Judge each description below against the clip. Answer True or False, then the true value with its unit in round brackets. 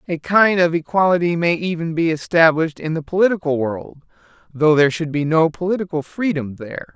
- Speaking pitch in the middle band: True (165 Hz)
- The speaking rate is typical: True (175 wpm)